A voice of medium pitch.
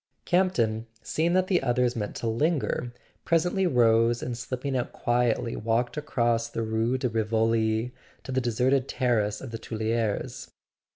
No: low, 120 Hz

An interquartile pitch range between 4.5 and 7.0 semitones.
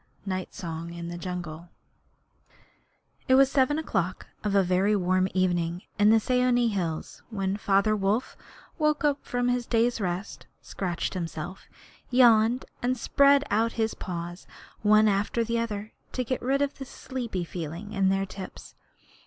Yes: average, 5.0 semitones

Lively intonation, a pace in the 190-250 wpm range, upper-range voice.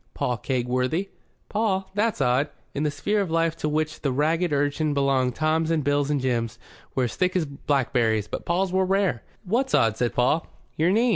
No: wide, 5.9 semitones; average, 195 wpm; medium, 150 Hz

